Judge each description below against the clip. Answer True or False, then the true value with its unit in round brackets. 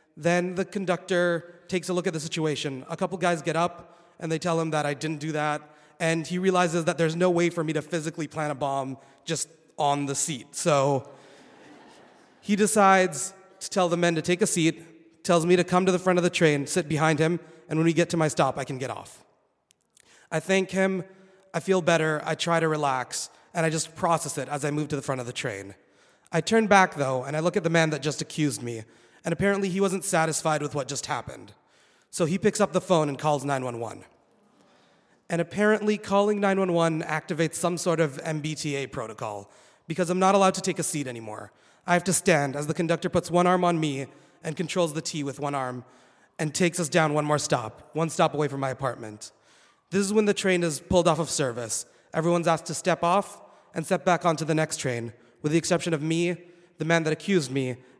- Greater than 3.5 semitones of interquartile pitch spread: False (3.2 semitones)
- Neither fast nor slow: False (220 wpm)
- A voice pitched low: False (165 Hz)